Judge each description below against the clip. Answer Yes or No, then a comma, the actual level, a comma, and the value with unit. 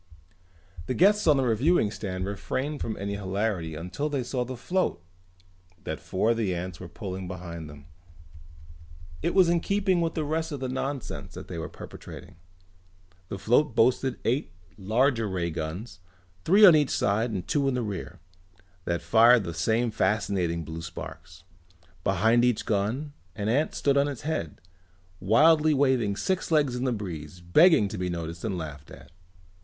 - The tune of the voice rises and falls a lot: Yes, wide, 7.4 semitones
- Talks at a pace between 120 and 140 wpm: No, average, 170 wpm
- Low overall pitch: Yes, low, 110 Hz